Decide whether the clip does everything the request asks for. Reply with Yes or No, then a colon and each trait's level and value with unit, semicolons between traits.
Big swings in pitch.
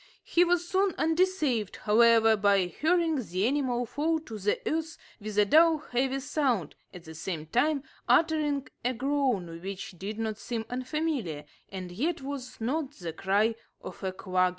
Yes: wide, 7.3 semitones